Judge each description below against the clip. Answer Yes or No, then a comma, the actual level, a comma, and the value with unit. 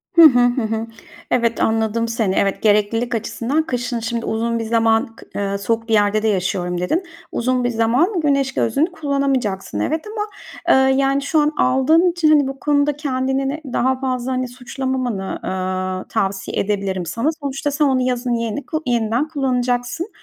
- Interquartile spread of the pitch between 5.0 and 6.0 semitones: No, average, 3.8 semitones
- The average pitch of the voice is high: Yes, high, 245 Hz